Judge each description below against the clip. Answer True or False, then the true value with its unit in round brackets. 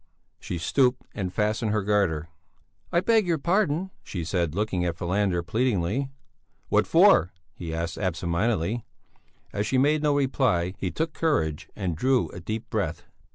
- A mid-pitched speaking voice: False (105 Hz)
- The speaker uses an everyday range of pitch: False (7.5 semitones)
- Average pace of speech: True (155 wpm)